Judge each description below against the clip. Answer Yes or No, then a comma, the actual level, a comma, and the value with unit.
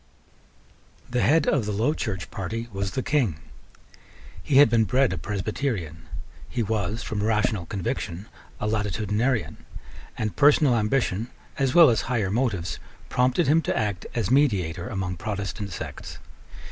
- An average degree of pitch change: Yes, average, 4.5 semitones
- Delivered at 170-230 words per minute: No, average, 145 wpm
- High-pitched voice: No, low, 110 Hz